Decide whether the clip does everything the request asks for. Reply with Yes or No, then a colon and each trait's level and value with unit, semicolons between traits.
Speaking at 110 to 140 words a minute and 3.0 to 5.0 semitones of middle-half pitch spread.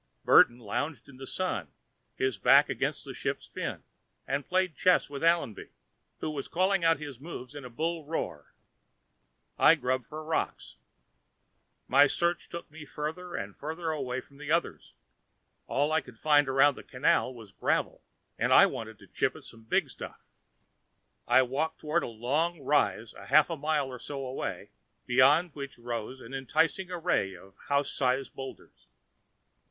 No: average, 165 wpm; average, 4.0 semitones